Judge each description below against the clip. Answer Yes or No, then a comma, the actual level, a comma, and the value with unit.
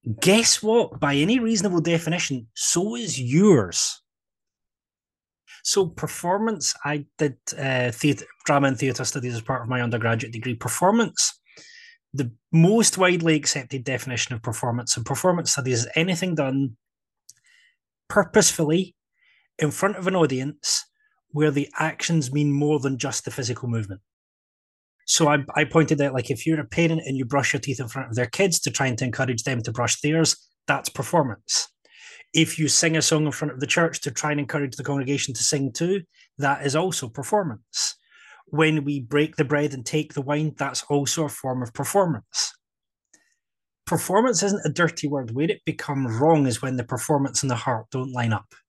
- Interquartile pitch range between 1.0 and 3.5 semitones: No, average, 4.3 semitones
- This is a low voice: No, medium, 145 Hz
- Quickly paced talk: No, average, 175 wpm